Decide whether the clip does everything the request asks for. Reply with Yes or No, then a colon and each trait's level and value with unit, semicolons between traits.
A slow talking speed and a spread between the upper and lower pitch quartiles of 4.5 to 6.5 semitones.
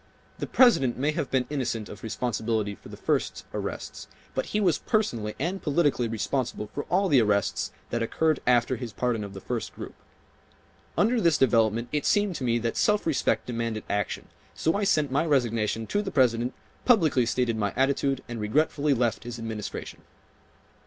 No: average, 175 wpm; average, 5.1 semitones